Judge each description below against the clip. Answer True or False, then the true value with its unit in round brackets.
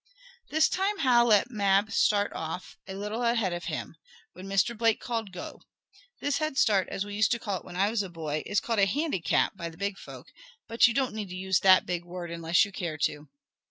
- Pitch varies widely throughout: False (4.3 semitones)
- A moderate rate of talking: False (230 wpm)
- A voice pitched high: True (200 Hz)